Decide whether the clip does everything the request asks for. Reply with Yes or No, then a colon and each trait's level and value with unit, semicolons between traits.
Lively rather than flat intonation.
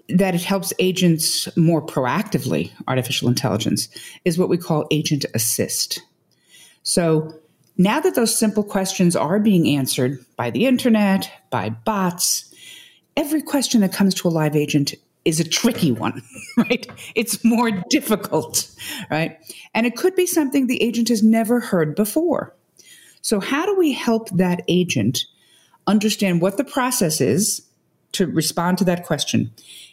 Yes: wide, 6.4 semitones